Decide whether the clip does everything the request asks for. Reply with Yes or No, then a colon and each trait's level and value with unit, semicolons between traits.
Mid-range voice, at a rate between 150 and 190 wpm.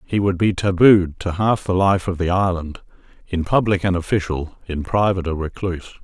No: very low, 90 Hz; average, 180 wpm